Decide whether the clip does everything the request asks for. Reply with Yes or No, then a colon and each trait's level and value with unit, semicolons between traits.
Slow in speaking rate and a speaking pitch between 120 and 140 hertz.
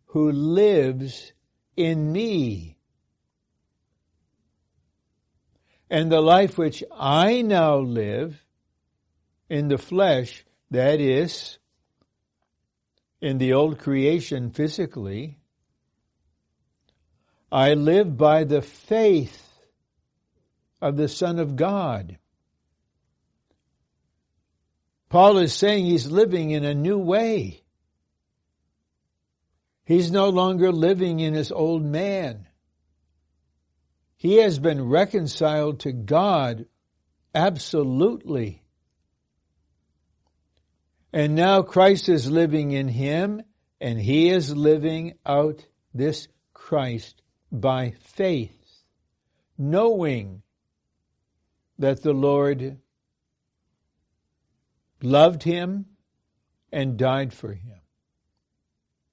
Yes: slow, 80 wpm; low, 135 Hz